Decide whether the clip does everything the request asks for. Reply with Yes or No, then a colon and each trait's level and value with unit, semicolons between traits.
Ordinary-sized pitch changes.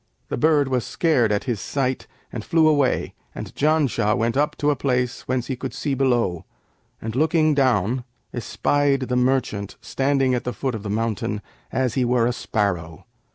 Yes: average, 3.4 semitones